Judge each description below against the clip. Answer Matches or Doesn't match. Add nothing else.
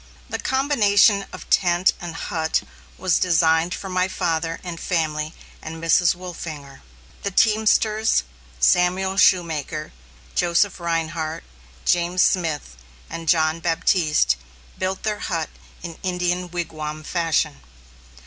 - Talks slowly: Matches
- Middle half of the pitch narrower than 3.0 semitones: Matches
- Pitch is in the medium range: Matches